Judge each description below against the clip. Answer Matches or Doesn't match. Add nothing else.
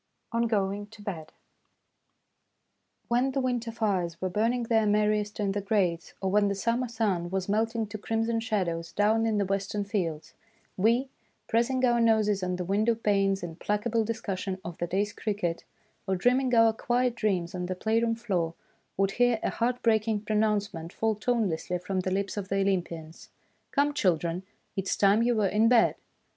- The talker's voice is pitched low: Doesn't match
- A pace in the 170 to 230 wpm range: Matches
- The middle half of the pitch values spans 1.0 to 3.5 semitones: Matches